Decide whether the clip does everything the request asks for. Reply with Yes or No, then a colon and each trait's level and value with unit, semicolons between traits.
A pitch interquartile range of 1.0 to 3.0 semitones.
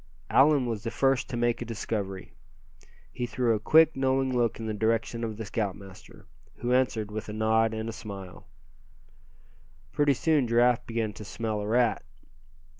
Yes: narrow, 2.4 semitones